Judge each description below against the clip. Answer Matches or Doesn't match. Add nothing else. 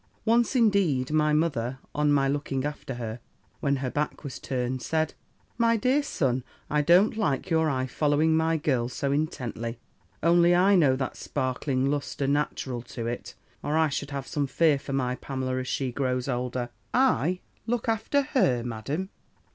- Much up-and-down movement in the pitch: Doesn't match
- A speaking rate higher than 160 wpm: Matches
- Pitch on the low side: Doesn't match